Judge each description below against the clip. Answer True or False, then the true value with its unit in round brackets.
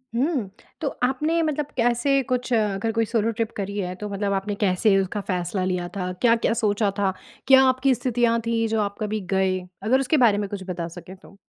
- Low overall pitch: False (215 Hz)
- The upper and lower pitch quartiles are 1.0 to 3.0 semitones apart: False (3.9 semitones)